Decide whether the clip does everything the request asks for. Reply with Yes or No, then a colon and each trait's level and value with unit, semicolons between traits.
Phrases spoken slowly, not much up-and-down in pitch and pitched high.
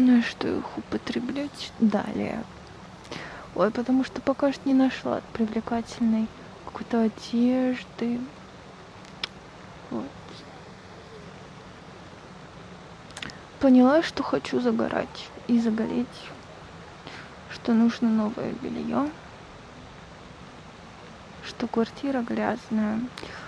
Yes: slow, 75 wpm; narrow, 2.3 semitones; high, 235 Hz